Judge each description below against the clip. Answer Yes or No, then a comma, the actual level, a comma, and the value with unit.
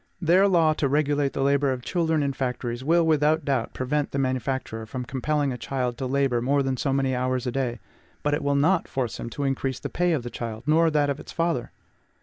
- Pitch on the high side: No, medium, 140 Hz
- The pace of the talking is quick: Yes, fast, 230 wpm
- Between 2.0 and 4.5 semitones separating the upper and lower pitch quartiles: Yes, average, 2.9 semitones